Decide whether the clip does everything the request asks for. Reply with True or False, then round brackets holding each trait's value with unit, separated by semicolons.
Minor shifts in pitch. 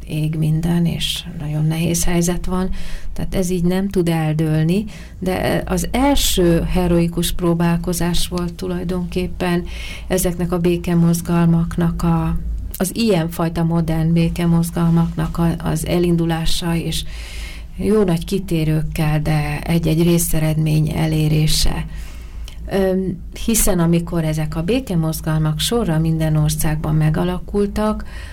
True (2.1 semitones)